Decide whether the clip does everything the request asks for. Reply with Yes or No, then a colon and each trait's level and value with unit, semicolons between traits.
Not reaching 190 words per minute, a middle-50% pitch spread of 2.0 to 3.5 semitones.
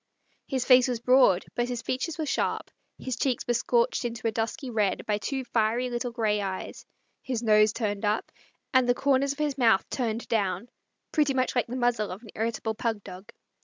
No: average, 200 wpm; average, 3.0 semitones